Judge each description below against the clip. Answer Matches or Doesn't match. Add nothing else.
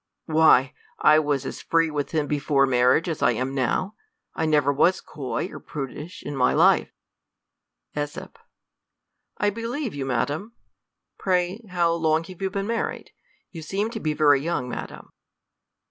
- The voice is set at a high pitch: Doesn't match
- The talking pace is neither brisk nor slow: Matches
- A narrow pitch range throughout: Doesn't match